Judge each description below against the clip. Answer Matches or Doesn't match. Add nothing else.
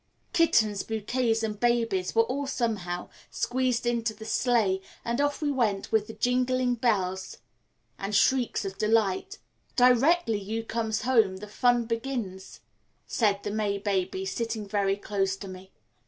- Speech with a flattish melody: Doesn't match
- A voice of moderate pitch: Doesn't match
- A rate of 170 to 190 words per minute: Doesn't match